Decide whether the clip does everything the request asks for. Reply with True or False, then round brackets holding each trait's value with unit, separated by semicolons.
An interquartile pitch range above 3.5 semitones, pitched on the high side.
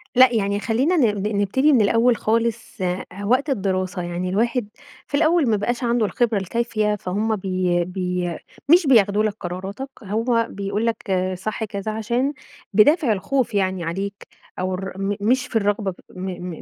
True (3.9 semitones; 210 Hz)